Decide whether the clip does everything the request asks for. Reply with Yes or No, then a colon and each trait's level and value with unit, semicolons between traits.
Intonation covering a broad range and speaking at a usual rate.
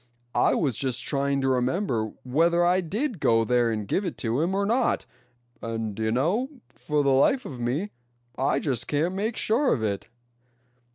Yes: wide, 7.4 semitones; average, 180 wpm